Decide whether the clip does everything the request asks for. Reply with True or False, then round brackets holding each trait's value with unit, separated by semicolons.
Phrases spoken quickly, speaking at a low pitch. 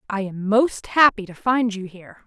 False (210 wpm; 210 Hz)